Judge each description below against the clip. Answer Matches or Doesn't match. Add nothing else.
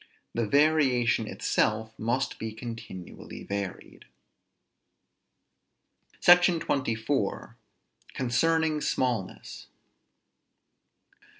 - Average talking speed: Doesn't match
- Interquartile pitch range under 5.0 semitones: Doesn't match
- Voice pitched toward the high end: Doesn't match